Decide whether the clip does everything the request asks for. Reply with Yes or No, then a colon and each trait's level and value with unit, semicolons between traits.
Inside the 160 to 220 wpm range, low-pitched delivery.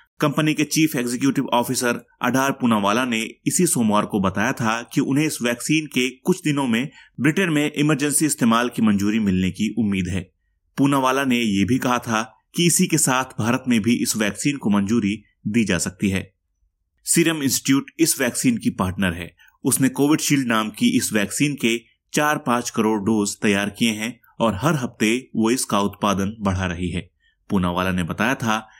Yes: average, 180 wpm; low, 120 Hz